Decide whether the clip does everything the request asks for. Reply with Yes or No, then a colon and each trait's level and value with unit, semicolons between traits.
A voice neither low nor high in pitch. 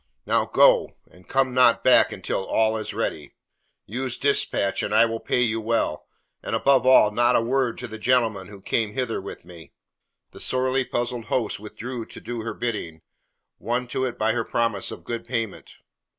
No: low, 115 Hz